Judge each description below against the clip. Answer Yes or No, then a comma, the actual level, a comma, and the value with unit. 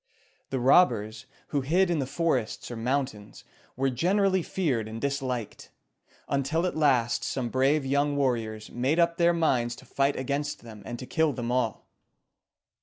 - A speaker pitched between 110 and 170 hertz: Yes, low, 135 Hz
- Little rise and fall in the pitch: No, average, 4.4 semitones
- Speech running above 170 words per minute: No, average, 160 wpm